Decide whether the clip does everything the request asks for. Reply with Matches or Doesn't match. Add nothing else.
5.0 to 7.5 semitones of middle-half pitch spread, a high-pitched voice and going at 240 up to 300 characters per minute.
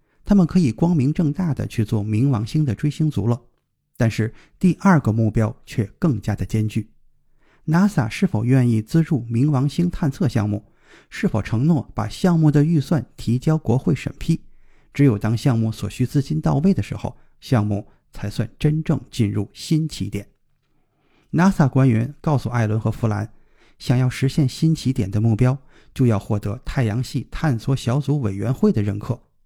Doesn't match